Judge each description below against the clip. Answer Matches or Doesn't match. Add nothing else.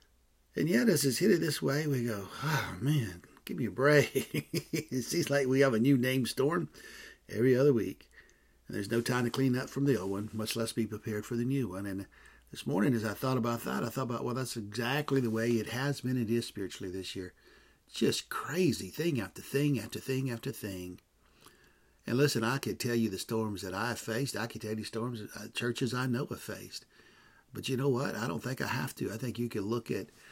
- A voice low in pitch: Matches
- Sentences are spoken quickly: Matches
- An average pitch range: Matches